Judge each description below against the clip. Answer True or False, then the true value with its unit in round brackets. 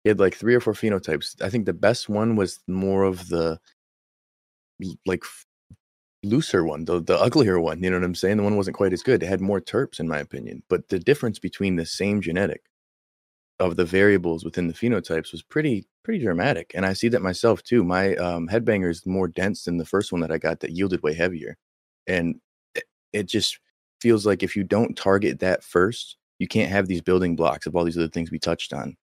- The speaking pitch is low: True (95 Hz)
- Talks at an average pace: False (220 wpm)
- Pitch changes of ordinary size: True (3.1 semitones)